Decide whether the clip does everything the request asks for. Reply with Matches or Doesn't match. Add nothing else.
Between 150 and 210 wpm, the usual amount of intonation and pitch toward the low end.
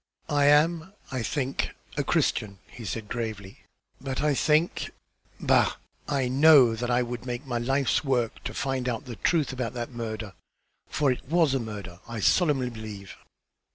Matches